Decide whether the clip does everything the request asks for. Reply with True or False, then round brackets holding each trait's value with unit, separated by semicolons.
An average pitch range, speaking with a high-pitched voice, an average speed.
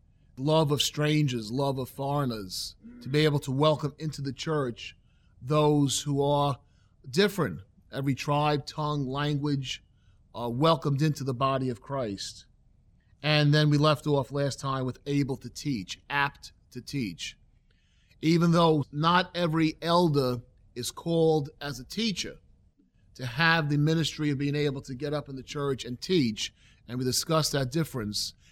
False (3.6 semitones; 140 Hz; 155 wpm)